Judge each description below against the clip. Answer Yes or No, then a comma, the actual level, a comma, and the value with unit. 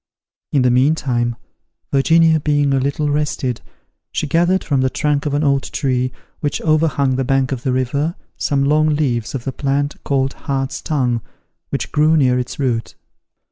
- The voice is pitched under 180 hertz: Yes, medium, 140 Hz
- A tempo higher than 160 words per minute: Yes, average, 170 wpm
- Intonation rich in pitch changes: No, narrow, 2.5 semitones